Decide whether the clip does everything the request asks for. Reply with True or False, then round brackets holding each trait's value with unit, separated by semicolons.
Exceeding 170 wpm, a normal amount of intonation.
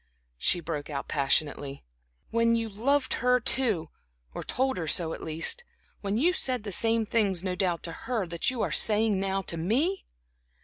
False (180 wpm; 6.1 semitones)